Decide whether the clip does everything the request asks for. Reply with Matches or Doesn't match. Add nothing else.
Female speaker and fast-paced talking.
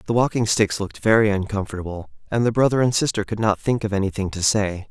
Doesn't match